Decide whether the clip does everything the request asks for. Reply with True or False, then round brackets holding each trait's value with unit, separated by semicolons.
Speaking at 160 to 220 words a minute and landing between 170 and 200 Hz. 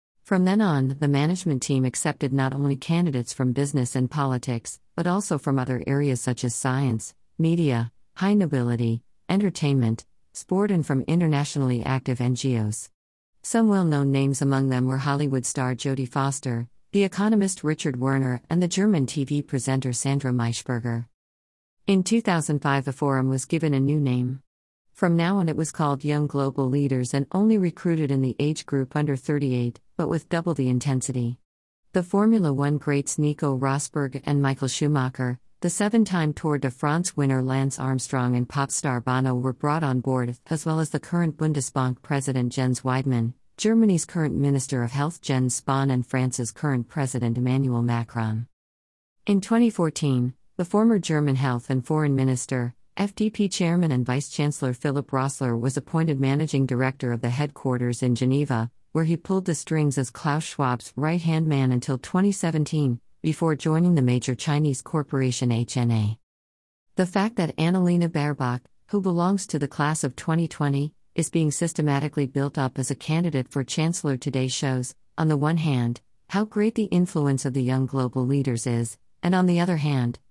False (165 wpm; 140 Hz)